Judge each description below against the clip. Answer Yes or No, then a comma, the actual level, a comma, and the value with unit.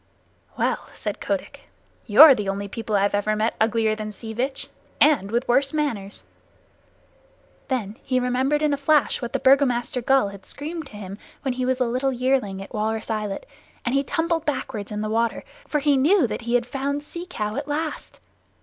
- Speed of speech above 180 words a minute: Yes, average, 190 wpm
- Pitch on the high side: Yes, very high, 250 Hz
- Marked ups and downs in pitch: No, average, 4.7 semitones